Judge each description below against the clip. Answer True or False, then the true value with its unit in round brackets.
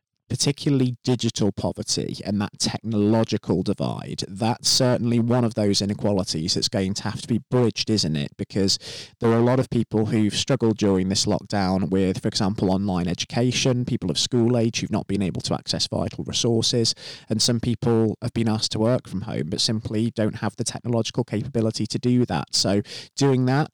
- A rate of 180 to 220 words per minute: True (185 wpm)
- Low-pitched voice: True (110 Hz)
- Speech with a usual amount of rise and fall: True (3.1 semitones)